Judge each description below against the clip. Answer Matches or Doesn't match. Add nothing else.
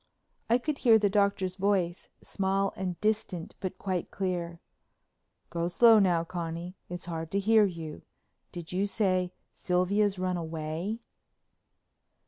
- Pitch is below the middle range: Doesn't match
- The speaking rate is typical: Doesn't match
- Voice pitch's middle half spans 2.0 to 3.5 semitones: Matches